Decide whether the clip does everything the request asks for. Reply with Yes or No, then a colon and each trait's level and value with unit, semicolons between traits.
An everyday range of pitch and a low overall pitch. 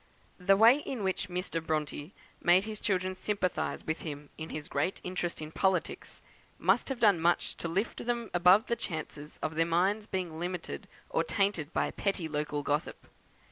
No: average, 3.7 semitones; medium, 180 Hz